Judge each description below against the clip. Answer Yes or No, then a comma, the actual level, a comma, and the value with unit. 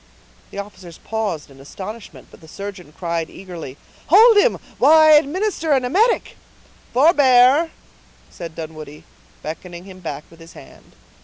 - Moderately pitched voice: No, high, 200 Hz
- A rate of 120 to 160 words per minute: Yes, average, 140 wpm